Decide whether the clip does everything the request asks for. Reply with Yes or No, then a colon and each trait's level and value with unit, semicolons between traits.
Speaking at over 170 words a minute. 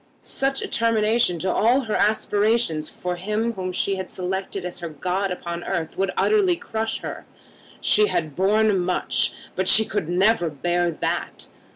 No: average, 165 wpm